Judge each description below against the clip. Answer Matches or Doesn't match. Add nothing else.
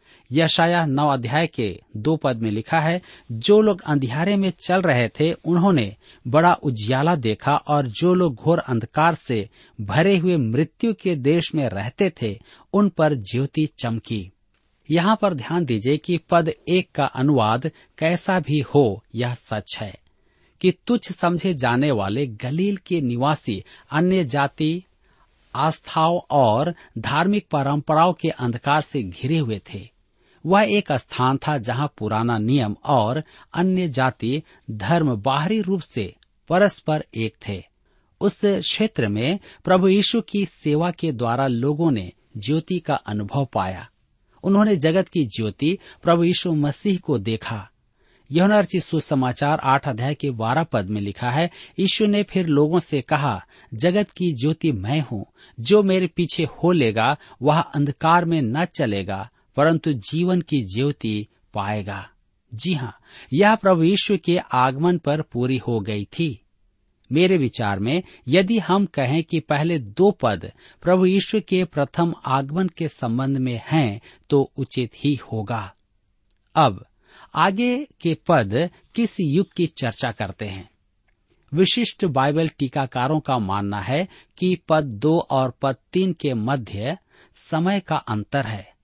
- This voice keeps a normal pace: Matches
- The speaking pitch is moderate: Matches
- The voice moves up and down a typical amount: Doesn't match